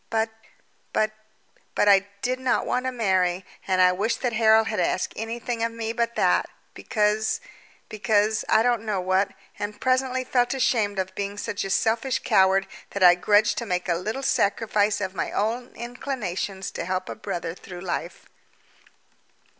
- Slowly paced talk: No, average, 170 wpm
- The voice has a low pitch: No, high, 210 Hz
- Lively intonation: No, average, 3.6 semitones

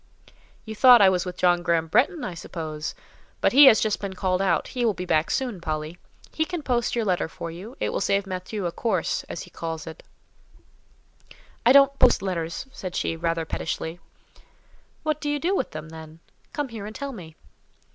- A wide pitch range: Yes, wide, 6.7 semitones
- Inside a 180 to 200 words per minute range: Yes, average, 195 wpm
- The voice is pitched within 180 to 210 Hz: Yes, high, 190 Hz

